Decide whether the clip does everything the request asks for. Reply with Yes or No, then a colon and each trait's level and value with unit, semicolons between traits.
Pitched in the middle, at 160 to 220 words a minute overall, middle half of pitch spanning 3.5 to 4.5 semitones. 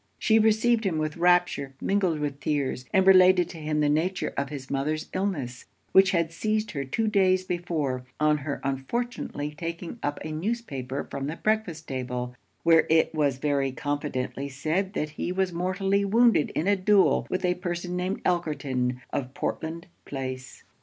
No: medium, 160 Hz; average, 165 wpm; average, 5.0 semitones